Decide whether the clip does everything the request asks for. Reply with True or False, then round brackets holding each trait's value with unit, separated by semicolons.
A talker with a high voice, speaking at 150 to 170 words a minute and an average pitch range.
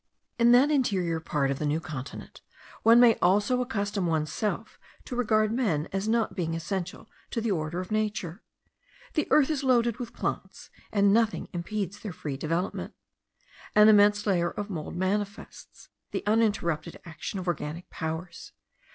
True (200 Hz; 155 wpm; 4.8 semitones)